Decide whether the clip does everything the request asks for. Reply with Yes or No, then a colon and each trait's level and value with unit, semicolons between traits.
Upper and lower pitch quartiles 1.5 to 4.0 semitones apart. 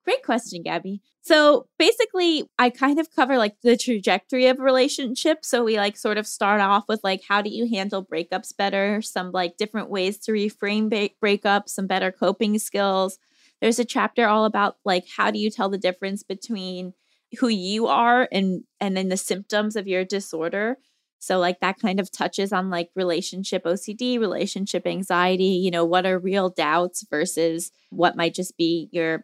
Yes: average, 3.6 semitones